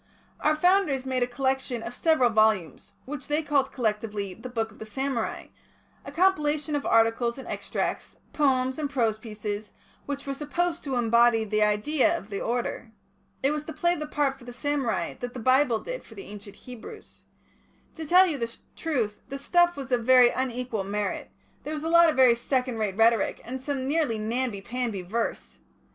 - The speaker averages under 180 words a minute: No, average, 185 wpm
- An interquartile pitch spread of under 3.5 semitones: No, average, 4.6 semitones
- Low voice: No, very high, 255 Hz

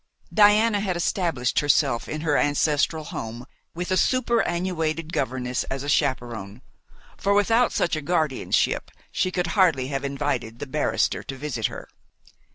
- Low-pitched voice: No, medium, 150 Hz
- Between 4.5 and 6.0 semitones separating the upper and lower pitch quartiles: Yes, wide, 5.4 semitones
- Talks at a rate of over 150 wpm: No, average, 145 wpm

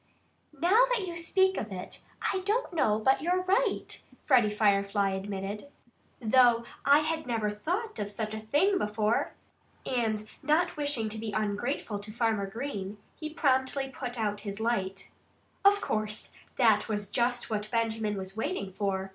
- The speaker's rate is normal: Yes, average, 155 wpm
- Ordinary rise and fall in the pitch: No, wide, 6.0 semitones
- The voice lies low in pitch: No, high, 225 Hz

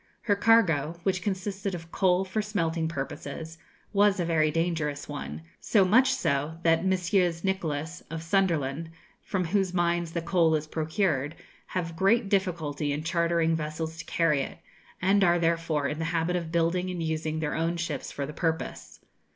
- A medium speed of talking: Yes, average, 165 wpm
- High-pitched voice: No, medium, 165 Hz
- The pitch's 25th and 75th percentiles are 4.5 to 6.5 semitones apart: No, average, 2.7 semitones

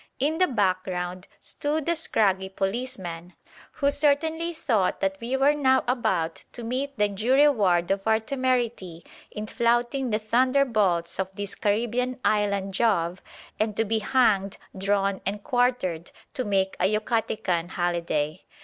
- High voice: Yes, high, 215 Hz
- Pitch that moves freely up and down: No, average, 5.0 semitones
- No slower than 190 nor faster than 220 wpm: No, average, 140 wpm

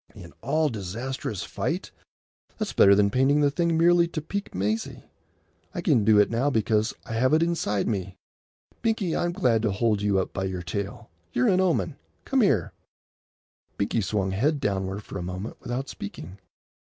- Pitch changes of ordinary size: No, wide, 7.0 semitones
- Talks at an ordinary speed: Yes, average, 175 wpm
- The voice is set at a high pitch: No, low, 110 Hz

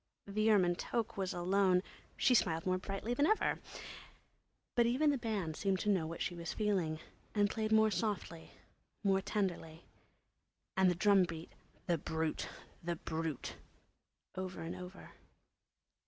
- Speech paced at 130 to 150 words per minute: Yes, average, 145 wpm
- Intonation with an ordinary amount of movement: Yes, average, 3.8 semitones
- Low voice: No, high, 190 Hz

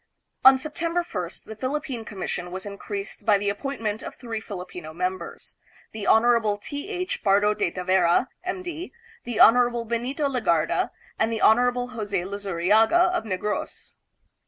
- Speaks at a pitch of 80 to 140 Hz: No, high, 220 Hz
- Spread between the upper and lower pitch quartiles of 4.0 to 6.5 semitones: Yes, average, 4.7 semitones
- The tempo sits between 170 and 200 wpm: No, average, 155 wpm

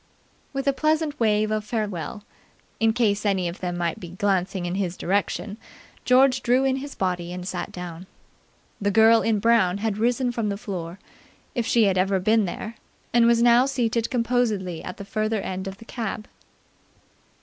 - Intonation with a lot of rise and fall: No, average, 3.9 semitones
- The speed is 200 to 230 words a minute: No, average, 180 wpm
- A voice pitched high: Yes, high, 215 Hz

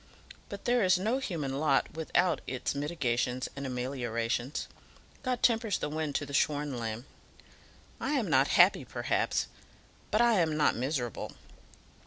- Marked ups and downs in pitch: Yes, wide, 6.3 semitones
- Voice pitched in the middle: Yes, medium, 145 Hz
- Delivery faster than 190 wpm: No, average, 145 wpm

